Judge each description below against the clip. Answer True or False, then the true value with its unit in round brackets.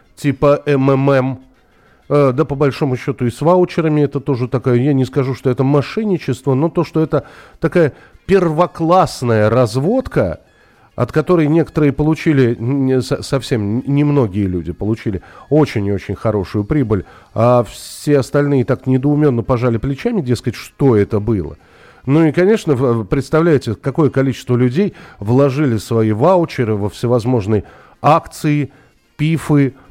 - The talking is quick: False (130 wpm)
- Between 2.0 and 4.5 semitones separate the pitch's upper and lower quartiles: True (3.9 semitones)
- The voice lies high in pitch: False (135 Hz)